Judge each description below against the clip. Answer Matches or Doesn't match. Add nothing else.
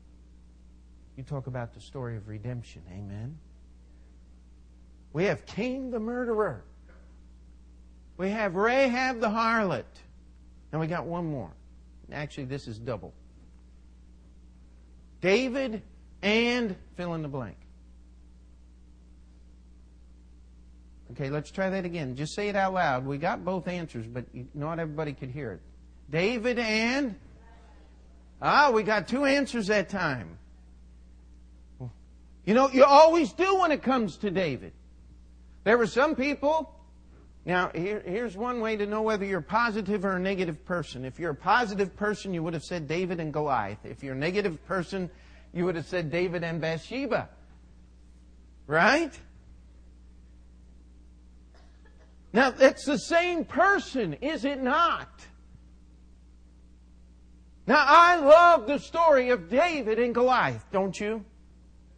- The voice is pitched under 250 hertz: Matches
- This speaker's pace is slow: Matches